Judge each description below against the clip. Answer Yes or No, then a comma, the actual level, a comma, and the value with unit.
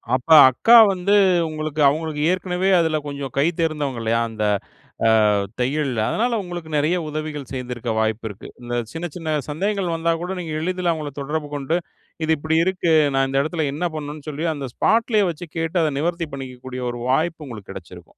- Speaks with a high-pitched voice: No, medium, 155 Hz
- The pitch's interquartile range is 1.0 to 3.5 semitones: No, average, 4.2 semitones